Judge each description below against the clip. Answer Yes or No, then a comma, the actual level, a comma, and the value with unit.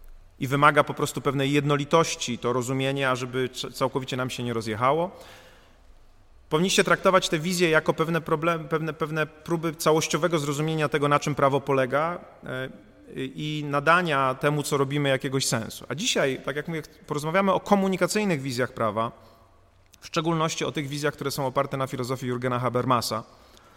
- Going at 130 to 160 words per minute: Yes, average, 150 wpm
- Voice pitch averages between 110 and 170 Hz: Yes, medium, 140 Hz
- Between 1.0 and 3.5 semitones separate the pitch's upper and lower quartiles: No, average, 4.0 semitones